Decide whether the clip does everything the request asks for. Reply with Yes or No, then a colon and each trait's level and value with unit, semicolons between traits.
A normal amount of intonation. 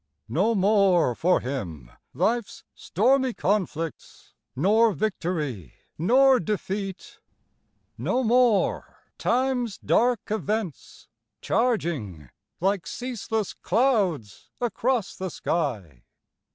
No: wide, 6.4 semitones